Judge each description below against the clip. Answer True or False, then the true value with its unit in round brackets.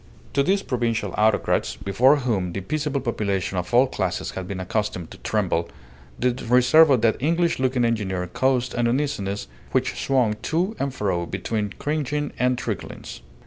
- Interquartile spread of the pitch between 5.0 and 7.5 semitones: True (5.5 semitones)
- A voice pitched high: False (120 Hz)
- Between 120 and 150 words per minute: False (160 wpm)